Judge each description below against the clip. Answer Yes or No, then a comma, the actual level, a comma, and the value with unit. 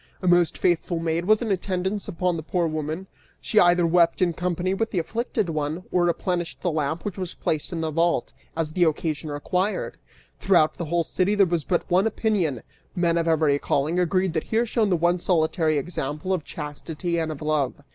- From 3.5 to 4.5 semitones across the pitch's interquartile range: No, narrow, 2.6 semitones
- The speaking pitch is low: No, medium, 170 Hz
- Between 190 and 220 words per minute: Yes, average, 200 wpm